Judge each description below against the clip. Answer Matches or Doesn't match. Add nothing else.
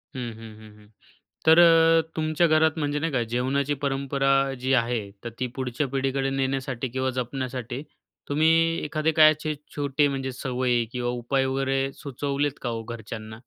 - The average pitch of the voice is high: Doesn't match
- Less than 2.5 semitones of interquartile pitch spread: Doesn't match